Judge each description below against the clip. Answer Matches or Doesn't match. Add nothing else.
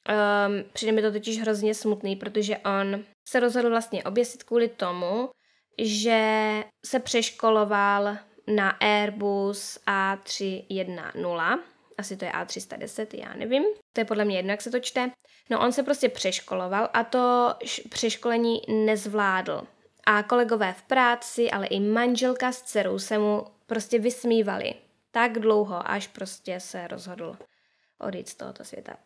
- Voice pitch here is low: Doesn't match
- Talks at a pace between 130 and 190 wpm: Matches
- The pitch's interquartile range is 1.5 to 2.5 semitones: Doesn't match